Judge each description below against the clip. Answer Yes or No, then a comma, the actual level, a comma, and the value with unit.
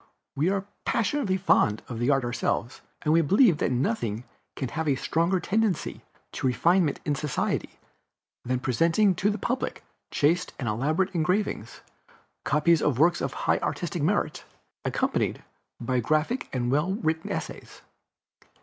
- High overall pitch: No, medium, 155 Hz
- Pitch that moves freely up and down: Yes, wide, 6.4 semitones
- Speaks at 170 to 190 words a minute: No, average, 140 wpm